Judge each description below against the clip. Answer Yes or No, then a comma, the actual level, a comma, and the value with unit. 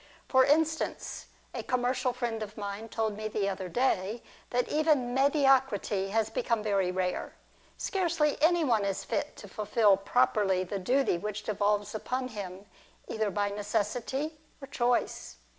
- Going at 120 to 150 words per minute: Yes, average, 145 wpm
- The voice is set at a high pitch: Yes, high, 220 Hz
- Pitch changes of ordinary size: Yes, average, 4.5 semitones